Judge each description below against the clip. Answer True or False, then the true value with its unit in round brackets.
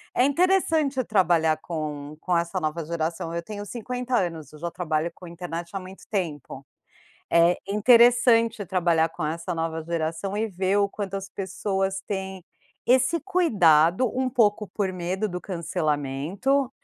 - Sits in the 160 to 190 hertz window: True (185 Hz)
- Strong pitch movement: False (4.7 semitones)